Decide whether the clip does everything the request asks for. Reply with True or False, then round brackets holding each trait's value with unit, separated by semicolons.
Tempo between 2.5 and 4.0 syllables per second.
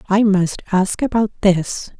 True (3.9 syllables/s)